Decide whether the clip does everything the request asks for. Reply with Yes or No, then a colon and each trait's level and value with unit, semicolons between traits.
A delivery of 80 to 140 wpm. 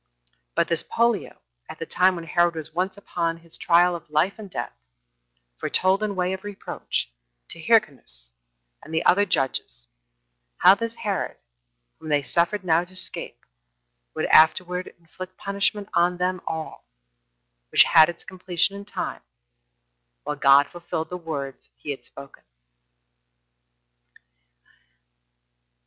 Yes: slow, 135 wpm